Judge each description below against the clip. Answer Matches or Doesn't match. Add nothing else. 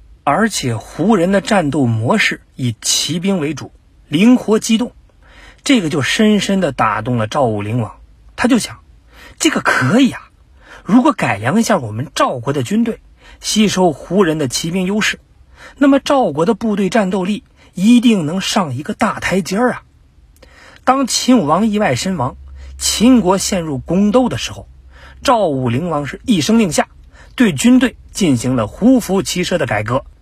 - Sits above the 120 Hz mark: Matches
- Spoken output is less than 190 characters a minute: Doesn't match